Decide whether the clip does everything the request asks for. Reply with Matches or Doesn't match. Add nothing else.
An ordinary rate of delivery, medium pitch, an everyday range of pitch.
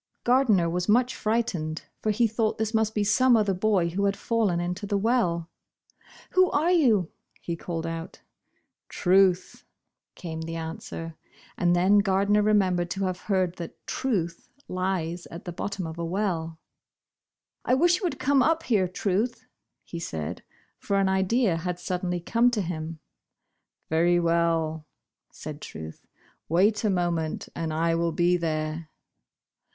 Matches